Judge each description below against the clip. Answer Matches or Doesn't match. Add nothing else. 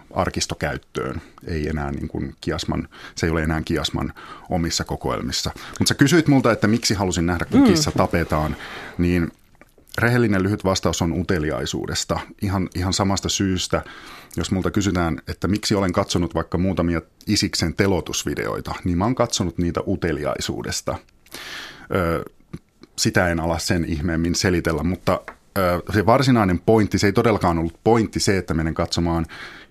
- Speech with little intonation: Doesn't match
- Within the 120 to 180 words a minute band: Matches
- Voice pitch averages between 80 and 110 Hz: Matches